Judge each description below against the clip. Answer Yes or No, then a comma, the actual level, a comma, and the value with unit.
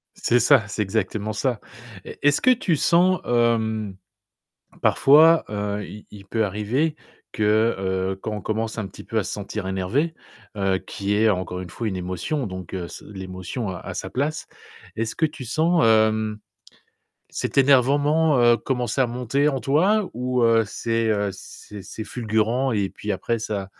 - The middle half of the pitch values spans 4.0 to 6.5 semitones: Yes, average, 4.7 semitones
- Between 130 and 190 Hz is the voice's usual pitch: No, low, 110 Hz